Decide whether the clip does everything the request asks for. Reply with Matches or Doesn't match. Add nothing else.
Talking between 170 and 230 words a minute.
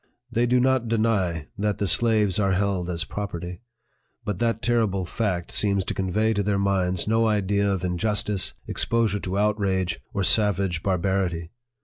Doesn't match